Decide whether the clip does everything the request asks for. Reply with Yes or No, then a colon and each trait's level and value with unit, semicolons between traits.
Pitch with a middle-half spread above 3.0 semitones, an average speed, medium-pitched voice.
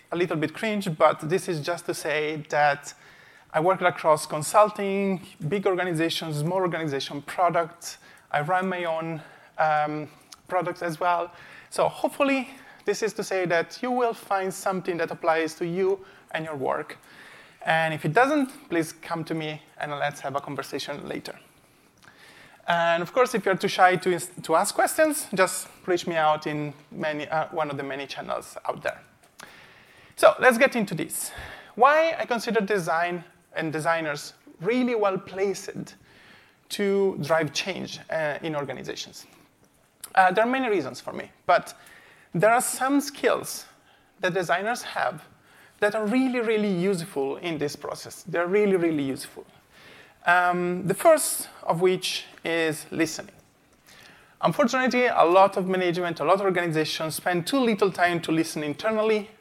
Yes: average, 4.2 semitones; average, 155 wpm; medium, 180 Hz